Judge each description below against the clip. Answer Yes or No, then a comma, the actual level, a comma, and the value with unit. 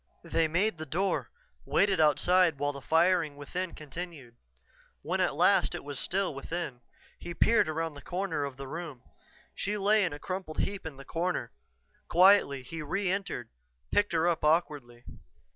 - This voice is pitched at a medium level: Yes, medium, 165 Hz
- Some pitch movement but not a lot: Yes, average, 4.2 semitones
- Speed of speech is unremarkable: Yes, average, 165 wpm